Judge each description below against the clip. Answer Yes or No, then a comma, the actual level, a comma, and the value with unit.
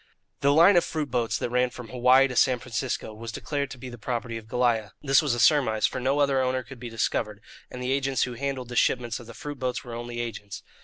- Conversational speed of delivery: No, fast, 250 wpm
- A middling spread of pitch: No, narrow, 2.3 semitones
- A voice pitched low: Yes, low, 125 Hz